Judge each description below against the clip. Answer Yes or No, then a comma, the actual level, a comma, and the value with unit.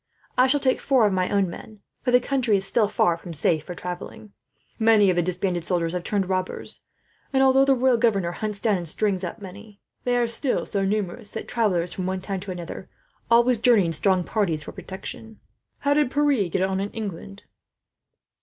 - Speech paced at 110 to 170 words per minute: No, fast, 205 wpm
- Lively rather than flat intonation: No, average, 4.3 semitones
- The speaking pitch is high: Yes, high, 200 Hz